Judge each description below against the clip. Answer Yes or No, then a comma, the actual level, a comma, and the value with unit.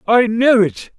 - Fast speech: No, average, 185 wpm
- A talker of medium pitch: No, high, 225 Hz